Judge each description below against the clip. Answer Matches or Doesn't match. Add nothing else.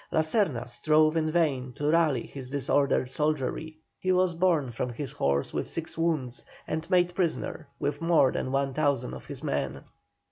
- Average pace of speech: Matches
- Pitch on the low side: Doesn't match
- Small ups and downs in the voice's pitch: Doesn't match